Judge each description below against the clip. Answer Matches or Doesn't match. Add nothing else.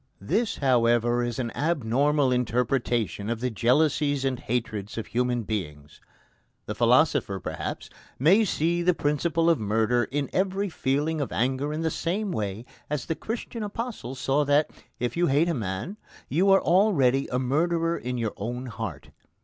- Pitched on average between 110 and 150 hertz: Matches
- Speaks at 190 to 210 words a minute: Doesn't match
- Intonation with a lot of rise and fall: Matches